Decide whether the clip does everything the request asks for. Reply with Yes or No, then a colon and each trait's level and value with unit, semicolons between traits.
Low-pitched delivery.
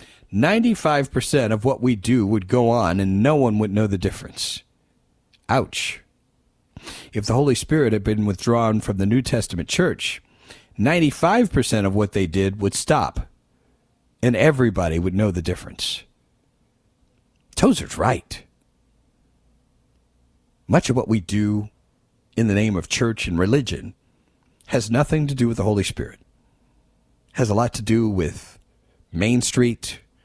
Yes: low, 110 Hz